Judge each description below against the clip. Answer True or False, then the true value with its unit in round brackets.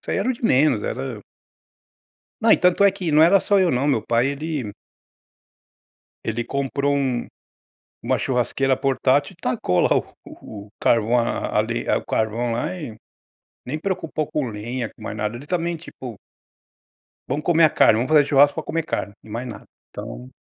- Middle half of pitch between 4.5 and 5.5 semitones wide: True (5.1 semitones)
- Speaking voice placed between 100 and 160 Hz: True (135 Hz)